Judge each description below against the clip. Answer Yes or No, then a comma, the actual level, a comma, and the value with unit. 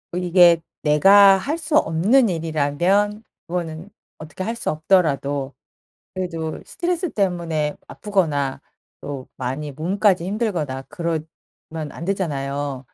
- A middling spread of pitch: Yes, average, 4.9 semitones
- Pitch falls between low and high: Yes, medium, 170 Hz